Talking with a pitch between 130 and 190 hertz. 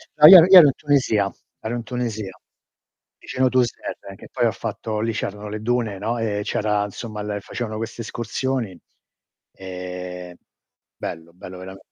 No: low, 110 Hz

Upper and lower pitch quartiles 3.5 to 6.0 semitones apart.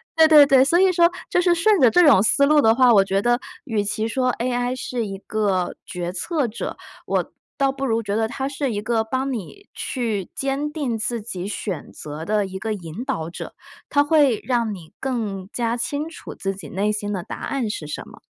Yes: average, 5.2 semitones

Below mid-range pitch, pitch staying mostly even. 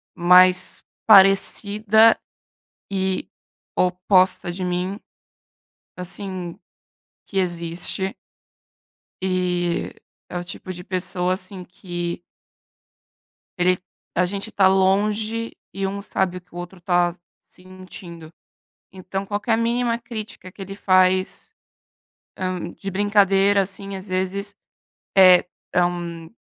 No: medium, 185 Hz; narrow, 1.8 semitones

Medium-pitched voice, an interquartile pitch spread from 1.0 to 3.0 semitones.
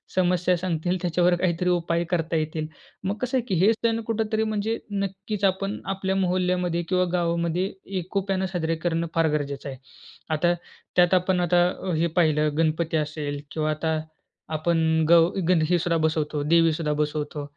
Yes: medium, 175 Hz; narrow, 2.6 semitones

